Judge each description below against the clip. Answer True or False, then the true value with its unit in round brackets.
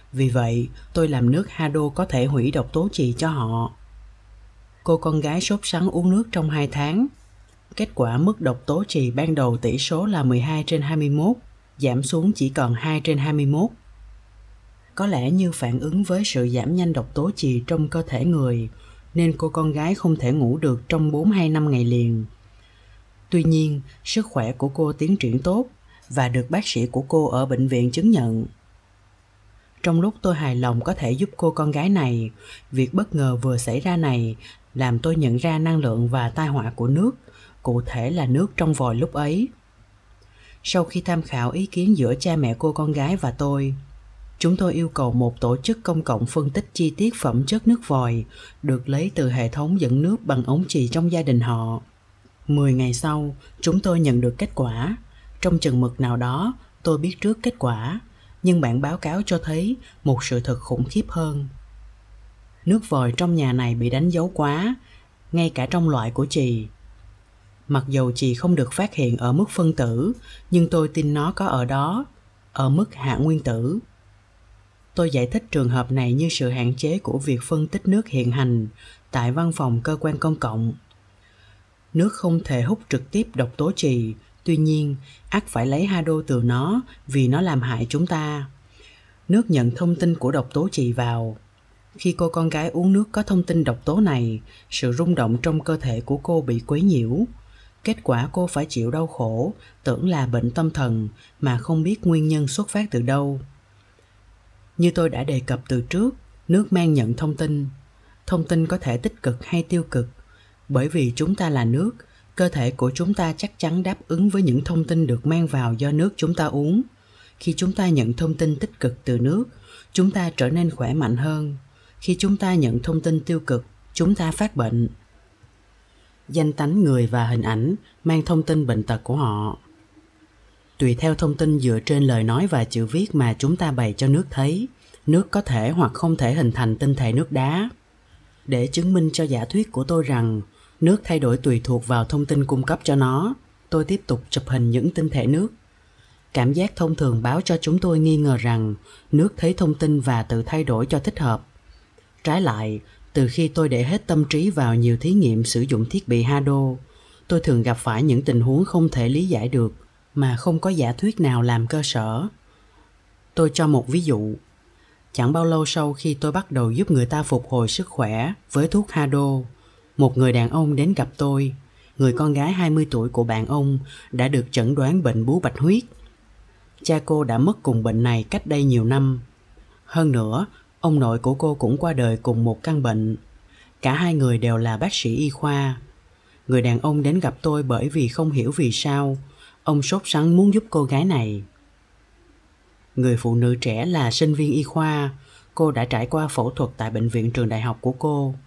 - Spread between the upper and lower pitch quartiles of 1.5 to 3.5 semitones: False (5.5 semitones)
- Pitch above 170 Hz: False (135 Hz)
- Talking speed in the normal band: True (205 wpm)